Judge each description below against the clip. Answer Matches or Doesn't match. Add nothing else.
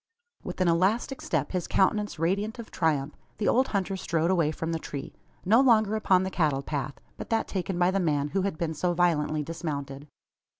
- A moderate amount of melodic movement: Matches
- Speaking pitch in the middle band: Matches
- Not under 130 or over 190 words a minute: Doesn't match